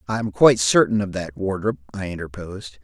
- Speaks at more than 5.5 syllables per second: Yes, 6.1 syllables/s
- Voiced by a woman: No, male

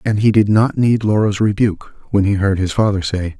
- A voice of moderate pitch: No, low, 105 Hz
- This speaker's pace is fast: Yes, fast, 230 wpm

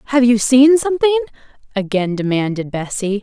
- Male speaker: No, female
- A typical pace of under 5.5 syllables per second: No, 5.6 syllables/s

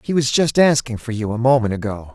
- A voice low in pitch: Yes, low, 120 Hz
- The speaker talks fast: Yes, fast, 250 wpm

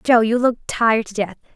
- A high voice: Yes, high, 225 Hz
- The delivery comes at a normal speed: No, fast, 230 wpm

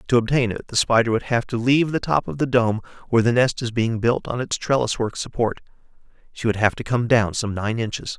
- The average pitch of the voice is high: No, low, 120 Hz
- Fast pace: Yes, fast, 250 wpm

